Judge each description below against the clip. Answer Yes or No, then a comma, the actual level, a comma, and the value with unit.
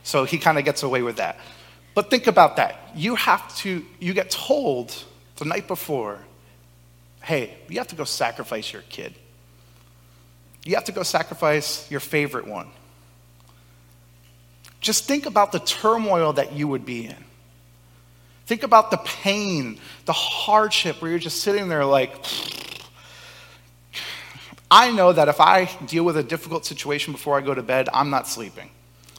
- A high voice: No, medium, 140 Hz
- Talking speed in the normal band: Yes, average, 160 wpm